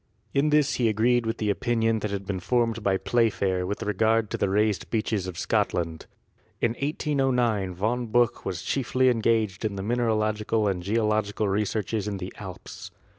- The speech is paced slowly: No, average, 165 wpm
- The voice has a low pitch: Yes, low, 110 Hz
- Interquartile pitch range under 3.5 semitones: Yes, average, 2.9 semitones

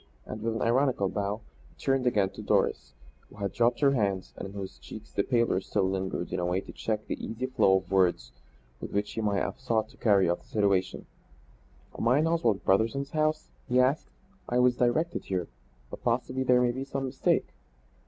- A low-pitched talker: Yes, low, 110 Hz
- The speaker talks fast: Yes, fast, 210 wpm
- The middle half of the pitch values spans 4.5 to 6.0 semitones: Yes, average, 4.8 semitones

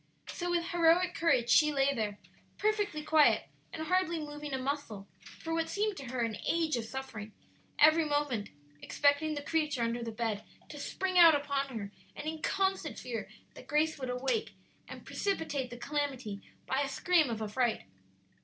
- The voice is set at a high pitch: Yes, very high, 290 Hz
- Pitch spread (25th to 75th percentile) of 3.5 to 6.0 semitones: Yes, average, 5.0 semitones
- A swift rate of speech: No, average, 175 wpm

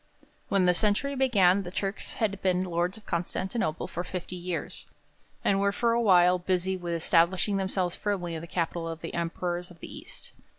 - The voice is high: No, medium, 180 Hz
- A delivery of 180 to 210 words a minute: Yes, average, 185 wpm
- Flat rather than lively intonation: Yes, narrow, 2.3 semitones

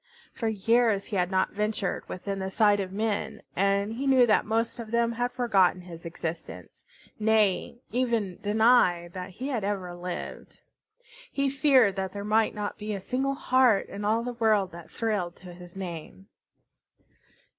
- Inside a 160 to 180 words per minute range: Yes, average, 165 wpm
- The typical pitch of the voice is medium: No, high, 210 Hz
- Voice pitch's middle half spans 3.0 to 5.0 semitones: Yes, average, 3.7 semitones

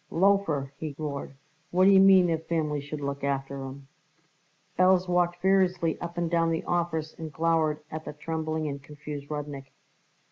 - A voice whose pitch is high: No, medium, 160 Hz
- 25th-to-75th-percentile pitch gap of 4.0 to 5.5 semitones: No, average, 3.2 semitones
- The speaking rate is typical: Yes, average, 165 wpm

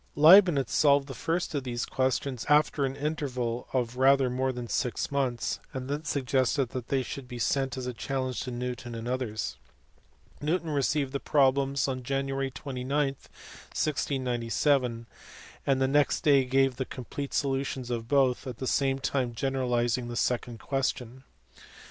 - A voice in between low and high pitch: No, low, 130 Hz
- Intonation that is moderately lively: No, narrow, 2.0 semitones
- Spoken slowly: No, average, 155 wpm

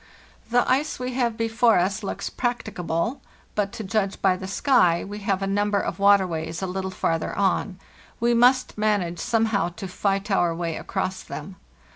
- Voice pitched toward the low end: No, high, 200 Hz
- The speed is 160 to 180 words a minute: Yes, average, 175 wpm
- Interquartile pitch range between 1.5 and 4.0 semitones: Yes, average, 3.6 semitones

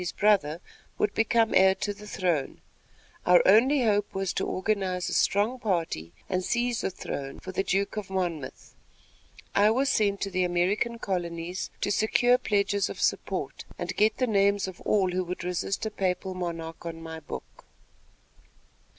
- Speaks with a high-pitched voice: Yes, high, 195 Hz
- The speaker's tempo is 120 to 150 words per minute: No, average, 165 wpm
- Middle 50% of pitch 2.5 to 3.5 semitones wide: Yes, average, 2.9 semitones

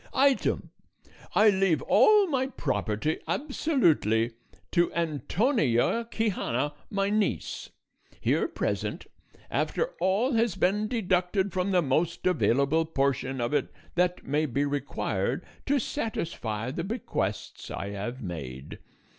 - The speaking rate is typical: No, slow, 115 wpm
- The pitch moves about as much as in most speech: No, wide, 8.4 semitones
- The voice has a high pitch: No, medium, 170 Hz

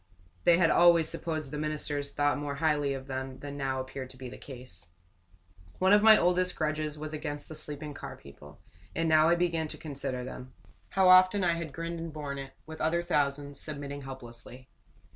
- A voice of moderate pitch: Yes, medium, 150 Hz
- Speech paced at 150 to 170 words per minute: No, average, 195 wpm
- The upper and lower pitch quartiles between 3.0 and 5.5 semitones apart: Yes, average, 3.4 semitones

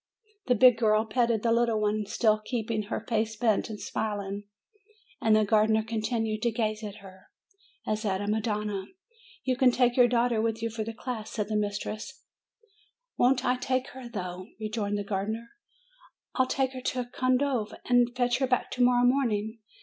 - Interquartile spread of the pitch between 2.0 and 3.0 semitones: Yes, narrow, 2.5 semitones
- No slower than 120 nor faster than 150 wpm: No, average, 185 wpm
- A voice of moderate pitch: No, high, 225 Hz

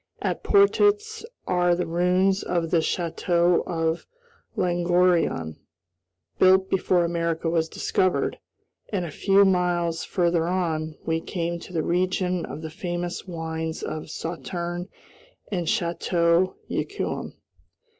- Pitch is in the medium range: Yes, medium, 175 Hz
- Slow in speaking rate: Yes, slow, 115 wpm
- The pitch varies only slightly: Yes, narrow, 1.7 semitones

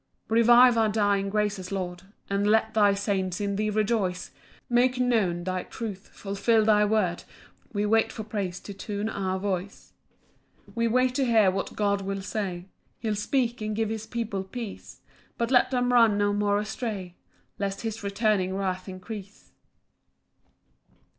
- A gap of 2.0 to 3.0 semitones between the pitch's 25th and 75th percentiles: Yes, narrow, 2.4 semitones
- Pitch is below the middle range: No, high, 205 Hz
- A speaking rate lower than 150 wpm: No, average, 160 wpm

